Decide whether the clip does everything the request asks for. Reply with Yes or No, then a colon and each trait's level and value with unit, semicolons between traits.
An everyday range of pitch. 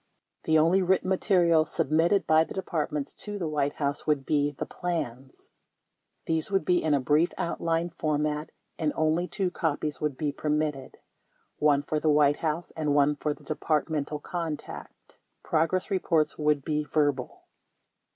No: narrow, 2.1 semitones